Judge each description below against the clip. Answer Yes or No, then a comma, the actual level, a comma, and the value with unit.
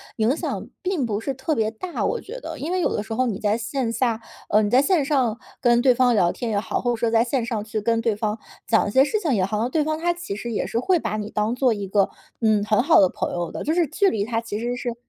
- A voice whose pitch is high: Yes, high, 235 Hz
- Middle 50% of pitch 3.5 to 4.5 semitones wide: Yes, average, 4.2 semitones